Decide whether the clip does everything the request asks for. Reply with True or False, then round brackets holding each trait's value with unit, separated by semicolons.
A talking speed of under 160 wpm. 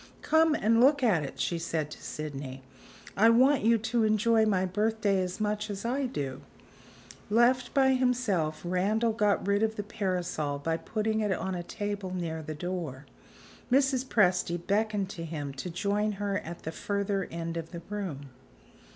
False (170 wpm)